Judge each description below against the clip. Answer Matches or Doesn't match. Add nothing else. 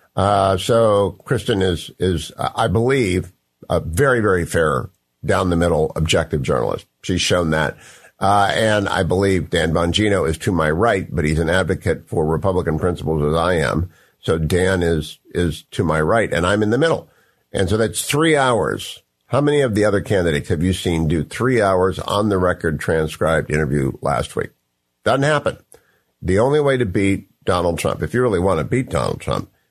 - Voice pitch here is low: Matches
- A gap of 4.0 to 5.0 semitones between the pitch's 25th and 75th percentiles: Matches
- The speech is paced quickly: Doesn't match